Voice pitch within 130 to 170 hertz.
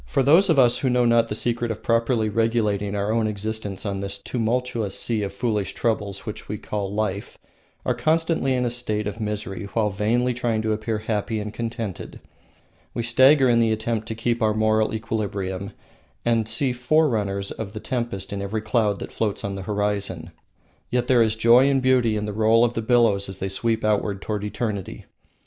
No: low, 110 Hz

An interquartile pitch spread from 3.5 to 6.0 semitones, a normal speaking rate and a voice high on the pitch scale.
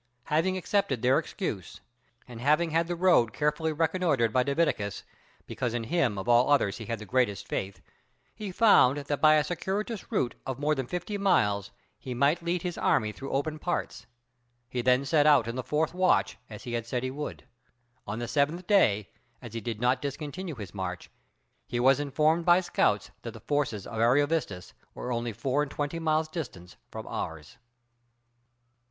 No: wide, 5.6 semitones; average, 185 wpm; medium, 140 Hz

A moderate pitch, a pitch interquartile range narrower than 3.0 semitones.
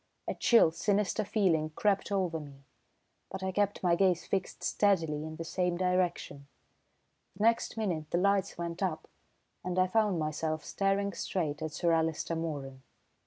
No: medium, 180 Hz; average, 3.6 semitones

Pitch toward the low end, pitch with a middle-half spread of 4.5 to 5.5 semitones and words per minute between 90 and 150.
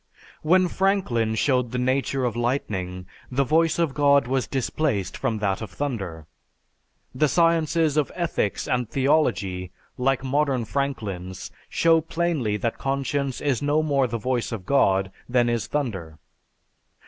Yes: low, 130 Hz; average, 4.8 semitones; average, 140 wpm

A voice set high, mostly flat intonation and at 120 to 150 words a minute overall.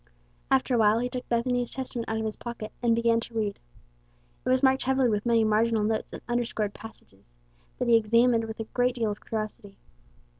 No: high, 230 Hz; narrow, 2.0 semitones; average, 195 wpm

